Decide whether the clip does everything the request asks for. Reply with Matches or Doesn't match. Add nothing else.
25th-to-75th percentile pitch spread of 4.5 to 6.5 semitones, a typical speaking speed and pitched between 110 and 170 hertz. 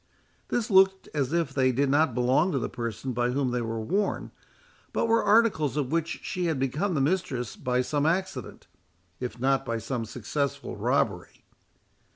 Matches